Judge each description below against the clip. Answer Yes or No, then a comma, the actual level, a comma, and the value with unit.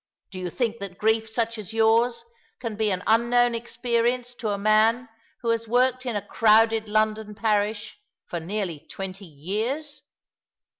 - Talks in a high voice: Yes, high, 220 Hz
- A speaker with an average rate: Yes, average, 155 wpm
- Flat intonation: Yes, narrow, 2.2 semitones